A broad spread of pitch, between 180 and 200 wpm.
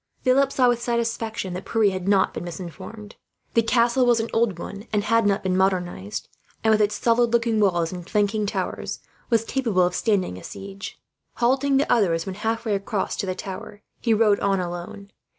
No: average, 3.5 semitones; average, 190 wpm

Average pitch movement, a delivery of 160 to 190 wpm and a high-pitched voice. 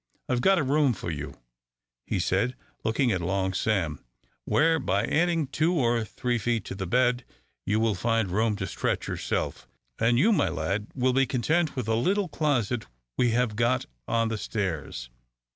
No: average, 4.5 semitones; average, 175 wpm; low, 120 Hz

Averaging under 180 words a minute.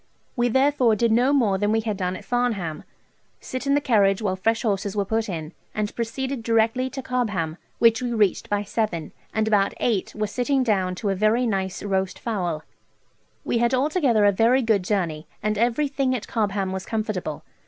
No: average, 195 wpm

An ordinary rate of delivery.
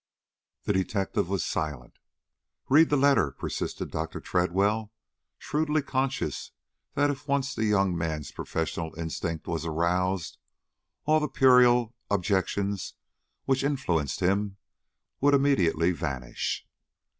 No: slow, 110 wpm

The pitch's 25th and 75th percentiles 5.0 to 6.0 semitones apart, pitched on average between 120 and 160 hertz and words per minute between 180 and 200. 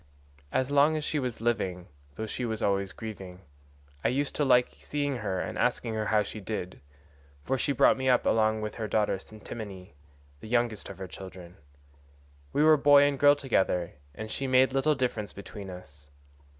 No: wide, 5.4 semitones; low, 110 Hz; average, 190 wpm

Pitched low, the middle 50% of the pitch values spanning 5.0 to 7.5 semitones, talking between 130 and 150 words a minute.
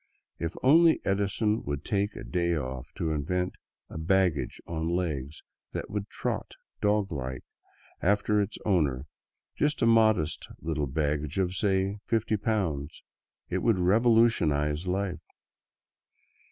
Yes: very low, 90 Hz; wide, 5.4 semitones; slow, 135 wpm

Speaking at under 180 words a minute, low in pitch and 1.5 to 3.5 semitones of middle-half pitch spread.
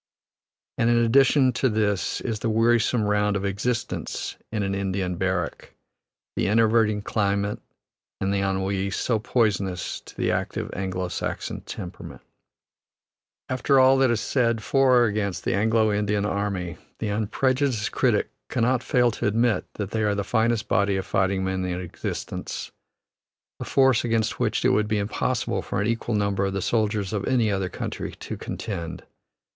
Yes: average, 160 wpm; low, 105 Hz; average, 3.0 semitones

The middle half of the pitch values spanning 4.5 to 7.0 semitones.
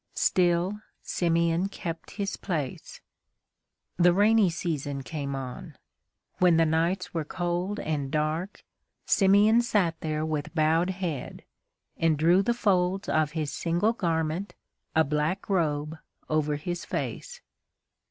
No: average, 3.4 semitones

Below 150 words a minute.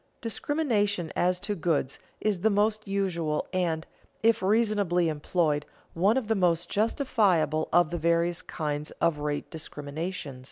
Yes: slow, 135 wpm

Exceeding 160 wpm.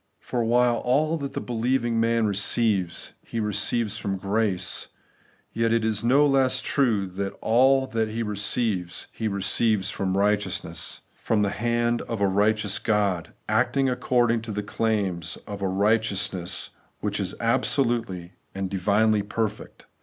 No: average, 145 wpm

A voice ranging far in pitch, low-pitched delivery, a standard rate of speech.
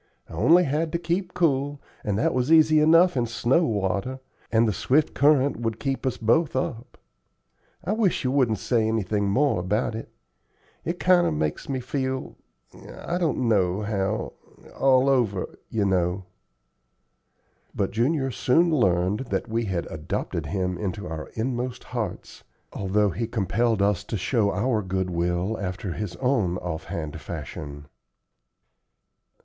Yes: wide, 6.0 semitones; low, 115 Hz; average, 150 wpm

